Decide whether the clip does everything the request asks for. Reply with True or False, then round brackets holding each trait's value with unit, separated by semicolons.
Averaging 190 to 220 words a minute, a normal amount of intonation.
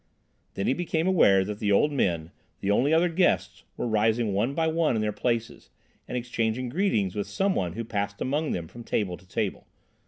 False (205 wpm; 6.7 semitones)